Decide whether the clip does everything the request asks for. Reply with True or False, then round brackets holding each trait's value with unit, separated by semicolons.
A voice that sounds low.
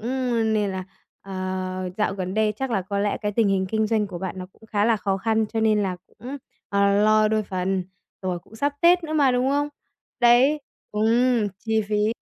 False (215 Hz)